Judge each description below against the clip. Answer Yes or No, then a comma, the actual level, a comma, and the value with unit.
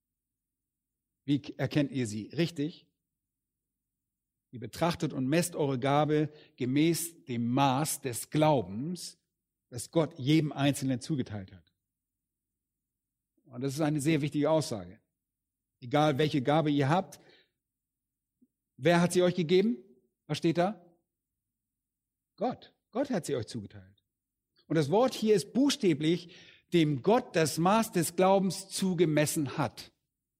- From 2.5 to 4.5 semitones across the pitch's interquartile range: No, average, 5.0 semitones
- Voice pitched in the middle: Yes, medium, 150 Hz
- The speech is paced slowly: Yes, slow, 120 wpm